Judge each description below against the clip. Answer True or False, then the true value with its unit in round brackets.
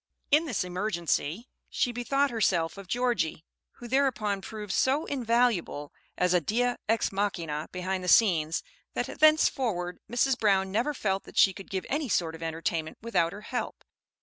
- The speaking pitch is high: True (200 Hz)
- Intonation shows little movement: False (5.6 semitones)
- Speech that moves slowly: False (160 wpm)